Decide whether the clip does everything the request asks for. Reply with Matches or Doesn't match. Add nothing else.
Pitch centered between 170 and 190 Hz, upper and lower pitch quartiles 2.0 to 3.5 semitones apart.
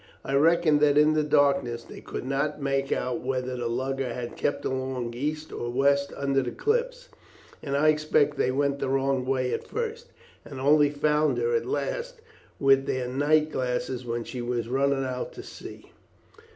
Doesn't match